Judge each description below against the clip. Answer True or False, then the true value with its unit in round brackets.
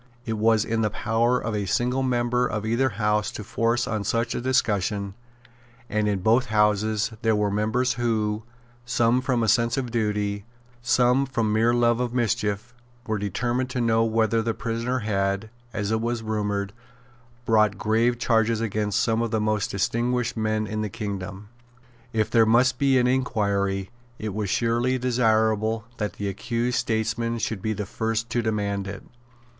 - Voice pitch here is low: True (110 Hz)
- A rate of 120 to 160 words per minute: False (170 wpm)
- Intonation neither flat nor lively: False (2.1 semitones)